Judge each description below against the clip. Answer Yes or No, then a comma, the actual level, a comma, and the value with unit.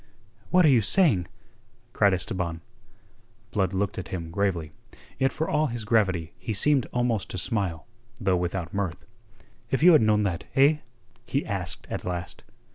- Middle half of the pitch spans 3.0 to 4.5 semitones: No, wide, 5.5 semitones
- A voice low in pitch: Yes, low, 100 Hz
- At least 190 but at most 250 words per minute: No, average, 160 wpm